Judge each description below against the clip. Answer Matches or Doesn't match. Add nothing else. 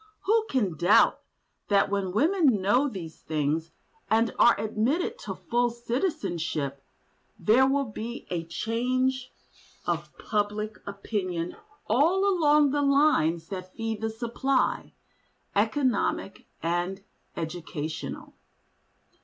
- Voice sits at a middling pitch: Doesn't match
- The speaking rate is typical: Doesn't match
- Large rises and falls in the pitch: Matches